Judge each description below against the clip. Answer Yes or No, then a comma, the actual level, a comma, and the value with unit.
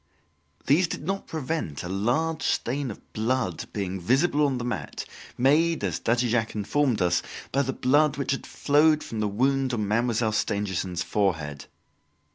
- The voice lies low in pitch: Yes, low, 120 Hz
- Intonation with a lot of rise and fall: Yes, wide, 6.1 semitones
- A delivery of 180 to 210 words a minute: No, average, 160 wpm